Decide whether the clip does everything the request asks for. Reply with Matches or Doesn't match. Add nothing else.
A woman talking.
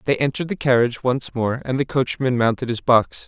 Doesn't match